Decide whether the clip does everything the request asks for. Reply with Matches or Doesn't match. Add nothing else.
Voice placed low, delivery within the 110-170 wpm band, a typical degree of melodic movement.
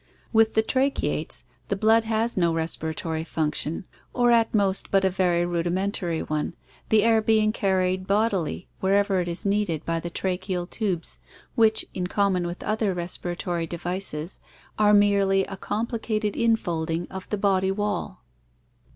Doesn't match